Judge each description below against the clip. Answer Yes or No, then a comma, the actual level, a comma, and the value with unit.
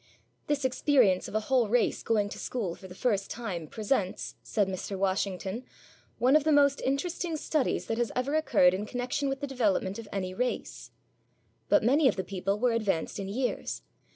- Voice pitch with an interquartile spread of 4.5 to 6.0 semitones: Yes, wide, 5.4 semitones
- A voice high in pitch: Yes, high, 230 Hz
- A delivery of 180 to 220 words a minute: Yes, average, 185 wpm